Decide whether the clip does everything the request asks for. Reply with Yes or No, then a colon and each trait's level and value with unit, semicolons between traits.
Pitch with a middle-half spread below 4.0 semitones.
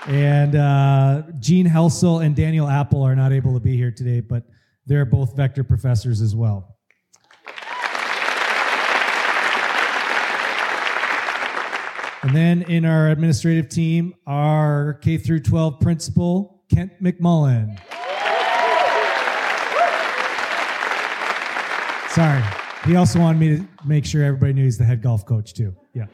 No: average, 4.5 semitones